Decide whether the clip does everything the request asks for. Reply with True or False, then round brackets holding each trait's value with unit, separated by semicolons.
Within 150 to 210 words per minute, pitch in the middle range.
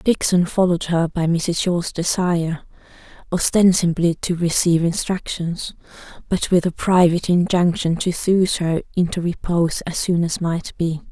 False (140 wpm; 175 Hz)